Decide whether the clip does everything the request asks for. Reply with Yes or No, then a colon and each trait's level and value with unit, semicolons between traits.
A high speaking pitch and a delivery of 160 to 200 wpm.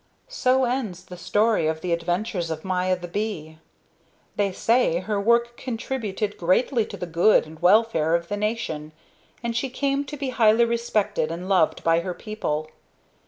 Yes: high, 200 Hz; average, 165 wpm